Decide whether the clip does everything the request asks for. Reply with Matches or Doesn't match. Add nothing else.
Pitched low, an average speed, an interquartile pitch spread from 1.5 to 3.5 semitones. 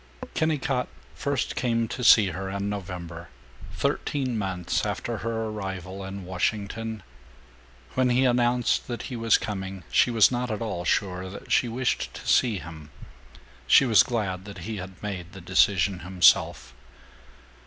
Doesn't match